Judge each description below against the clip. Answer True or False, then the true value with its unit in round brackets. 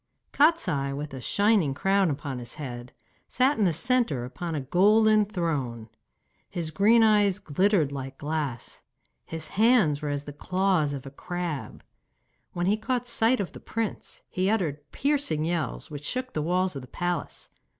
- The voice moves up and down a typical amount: False (6.6 semitones)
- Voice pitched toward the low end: False (175 Hz)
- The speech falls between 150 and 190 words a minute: True (165 wpm)